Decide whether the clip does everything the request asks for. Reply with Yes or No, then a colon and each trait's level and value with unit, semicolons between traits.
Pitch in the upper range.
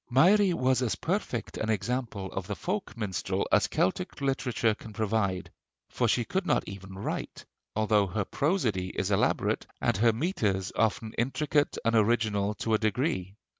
No: low, 110 Hz